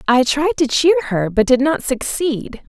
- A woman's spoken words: Yes, female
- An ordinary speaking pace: Yes, average, 195 wpm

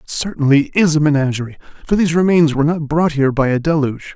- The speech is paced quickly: Yes, fast, 215 wpm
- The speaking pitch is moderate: Yes, medium, 150 Hz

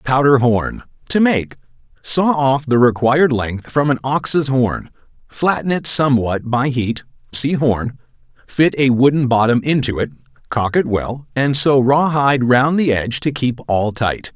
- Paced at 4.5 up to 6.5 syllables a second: No, 4.3 syllables/s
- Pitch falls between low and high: No, low, 130 Hz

